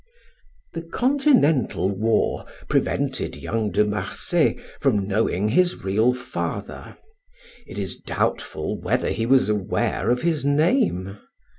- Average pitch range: No, wide, 7.7 semitones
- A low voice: Yes, low, 115 Hz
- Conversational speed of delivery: No, slow, 115 wpm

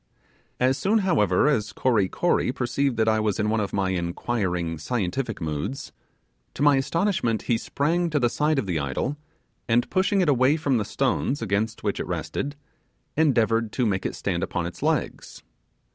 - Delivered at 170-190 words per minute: Yes, average, 175 wpm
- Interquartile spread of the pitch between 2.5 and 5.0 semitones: No, wide, 5.6 semitones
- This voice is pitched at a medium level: No, low, 120 Hz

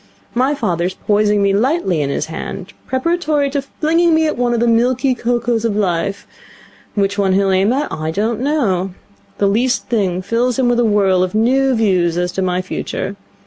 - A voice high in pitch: Yes, high, 220 Hz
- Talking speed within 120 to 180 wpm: No, average, 195 wpm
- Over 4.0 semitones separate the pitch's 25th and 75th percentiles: Yes, average, 5.1 semitones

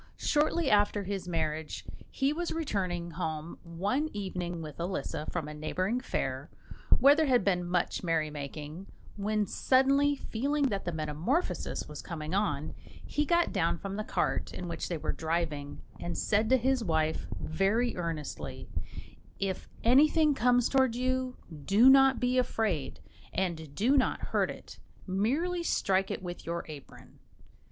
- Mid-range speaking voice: No, high, 195 Hz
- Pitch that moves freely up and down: Yes, wide, 7.6 semitones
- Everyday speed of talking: Yes, average, 150 wpm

